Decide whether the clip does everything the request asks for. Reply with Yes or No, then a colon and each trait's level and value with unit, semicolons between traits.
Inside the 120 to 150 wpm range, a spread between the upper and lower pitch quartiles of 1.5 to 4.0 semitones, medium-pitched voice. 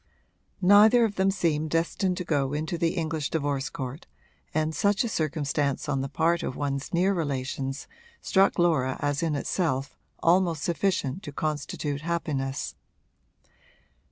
Yes: average, 140 wpm; average, 3.7 semitones; medium, 155 Hz